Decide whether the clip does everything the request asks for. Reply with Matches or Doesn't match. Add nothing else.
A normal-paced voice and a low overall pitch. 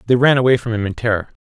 Doesn't match